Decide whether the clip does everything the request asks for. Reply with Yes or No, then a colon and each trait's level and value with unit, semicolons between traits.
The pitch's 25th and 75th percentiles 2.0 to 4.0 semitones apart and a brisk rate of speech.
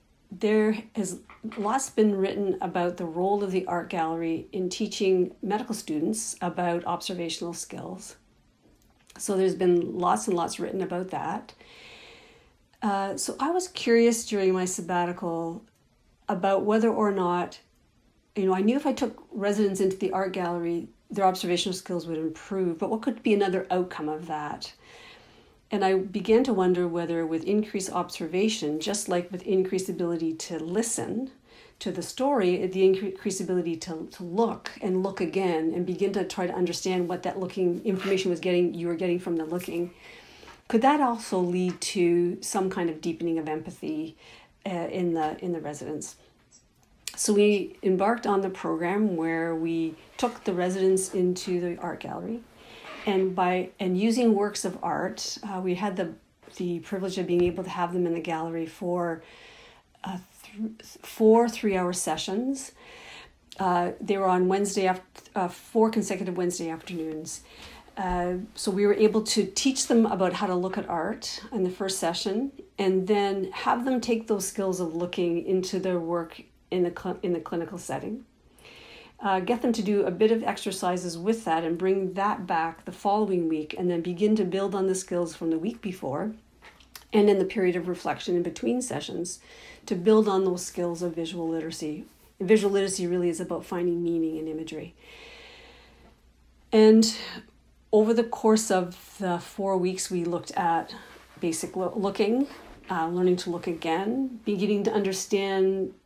No: average, 3.0 semitones; average, 170 wpm